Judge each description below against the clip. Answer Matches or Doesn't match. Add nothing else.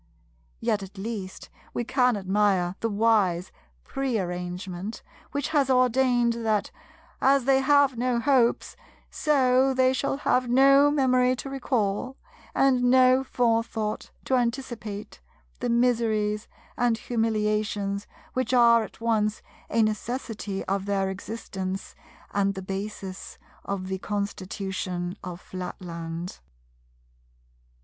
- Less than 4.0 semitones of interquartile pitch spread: Doesn't match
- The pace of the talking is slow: Matches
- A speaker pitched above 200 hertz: Matches